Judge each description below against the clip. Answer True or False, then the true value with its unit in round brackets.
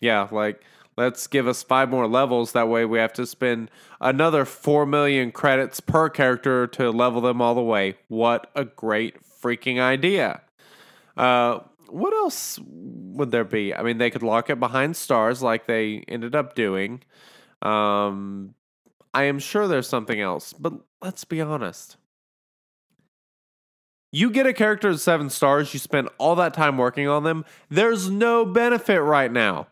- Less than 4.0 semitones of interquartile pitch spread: False (4.4 semitones)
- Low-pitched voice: True (130 Hz)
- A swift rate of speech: False (165 wpm)